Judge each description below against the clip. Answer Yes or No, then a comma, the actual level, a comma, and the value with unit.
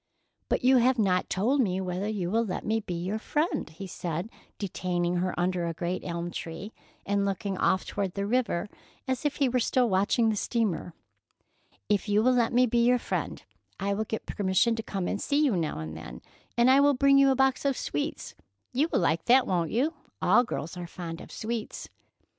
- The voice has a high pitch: Yes, high, 205 Hz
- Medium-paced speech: No, fast, 210 wpm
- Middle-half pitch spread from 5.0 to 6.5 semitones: Yes, wide, 5.5 semitones